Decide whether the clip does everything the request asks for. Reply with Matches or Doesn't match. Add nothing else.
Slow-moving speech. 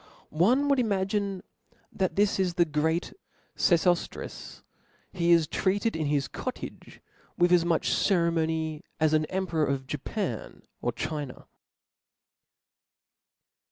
Matches